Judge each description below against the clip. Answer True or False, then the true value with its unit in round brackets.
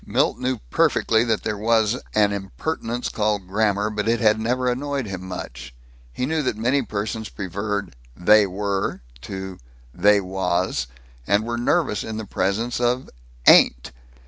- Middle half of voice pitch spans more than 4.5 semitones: False (3.3 semitones)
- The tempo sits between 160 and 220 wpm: False (150 wpm)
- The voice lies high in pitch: False (105 Hz)